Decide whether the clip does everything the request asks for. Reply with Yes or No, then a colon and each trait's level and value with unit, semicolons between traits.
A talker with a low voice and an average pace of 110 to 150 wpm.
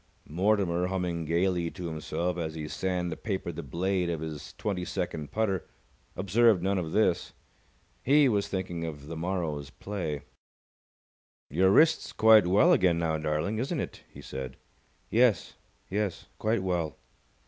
Yes: very low, 90 Hz; average, 145 wpm